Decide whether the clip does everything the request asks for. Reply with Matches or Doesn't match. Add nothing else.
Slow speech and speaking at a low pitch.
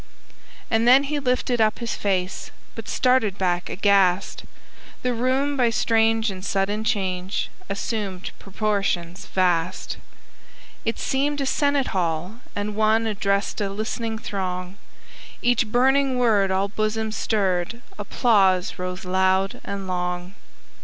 Doesn't match